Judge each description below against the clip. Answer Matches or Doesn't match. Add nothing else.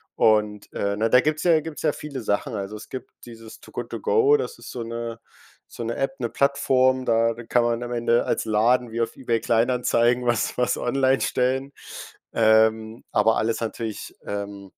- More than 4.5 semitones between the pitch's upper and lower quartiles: Doesn't match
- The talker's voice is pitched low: Matches